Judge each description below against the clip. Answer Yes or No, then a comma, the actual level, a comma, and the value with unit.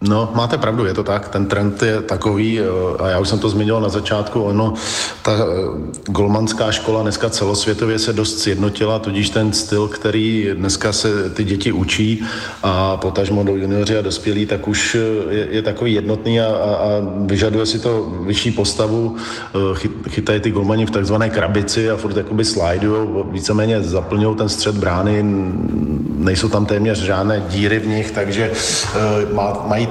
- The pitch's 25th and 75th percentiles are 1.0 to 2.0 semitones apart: Yes, narrow, 1.5 semitones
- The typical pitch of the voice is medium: No, low, 105 Hz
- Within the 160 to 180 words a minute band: Yes, average, 165 wpm